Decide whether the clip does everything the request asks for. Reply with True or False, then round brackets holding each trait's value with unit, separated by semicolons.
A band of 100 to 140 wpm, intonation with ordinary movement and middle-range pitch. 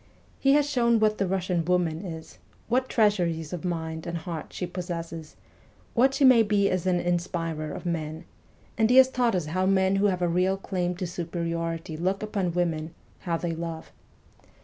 False (185 wpm; 3.0 semitones; 180 Hz)